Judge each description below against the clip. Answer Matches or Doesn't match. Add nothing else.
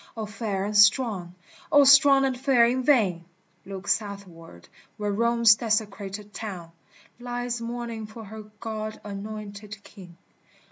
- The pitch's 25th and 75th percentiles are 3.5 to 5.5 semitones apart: Doesn't match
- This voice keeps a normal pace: Doesn't match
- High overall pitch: Matches